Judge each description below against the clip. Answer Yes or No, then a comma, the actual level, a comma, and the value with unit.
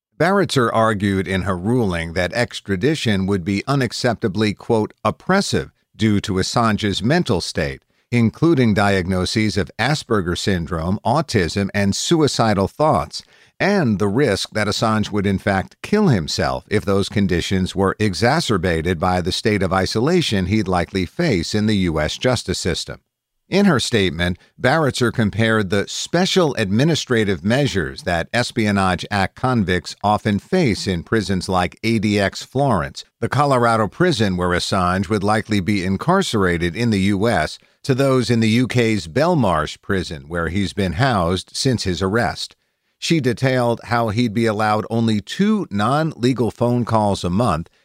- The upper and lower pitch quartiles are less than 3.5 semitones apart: No, average, 4.1 semitones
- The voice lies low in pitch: Yes, low, 105 Hz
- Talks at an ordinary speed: Yes, average, 145 wpm